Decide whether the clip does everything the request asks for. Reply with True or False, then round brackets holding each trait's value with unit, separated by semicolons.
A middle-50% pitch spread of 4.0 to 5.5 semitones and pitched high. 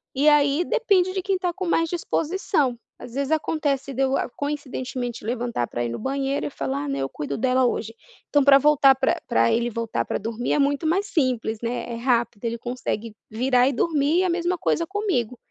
True (5.1 semitones; 270 Hz)